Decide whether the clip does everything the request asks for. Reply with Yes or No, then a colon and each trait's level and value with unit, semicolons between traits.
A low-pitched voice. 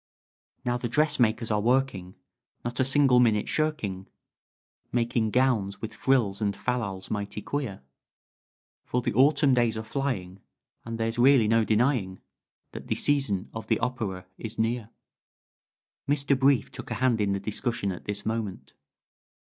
Yes: low, 115 Hz